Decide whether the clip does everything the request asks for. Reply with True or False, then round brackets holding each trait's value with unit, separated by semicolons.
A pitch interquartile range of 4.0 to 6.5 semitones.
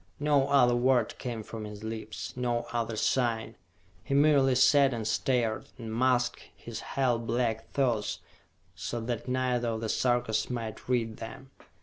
False (2.4 semitones)